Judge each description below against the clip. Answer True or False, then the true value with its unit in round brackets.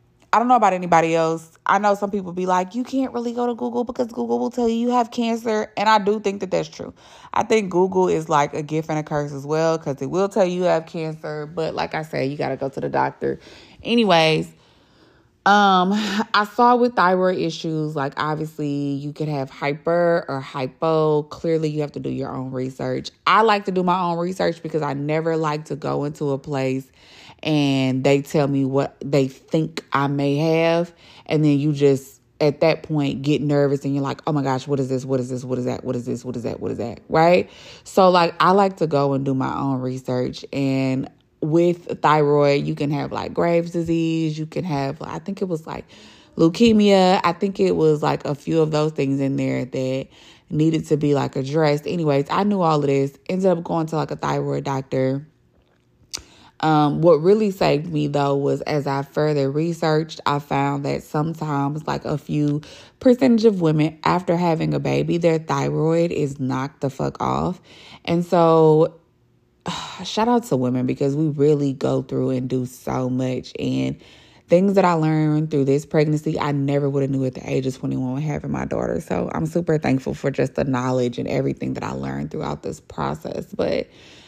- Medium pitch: True (150 Hz)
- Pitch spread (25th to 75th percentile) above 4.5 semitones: False (3.9 semitones)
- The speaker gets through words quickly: True (210 wpm)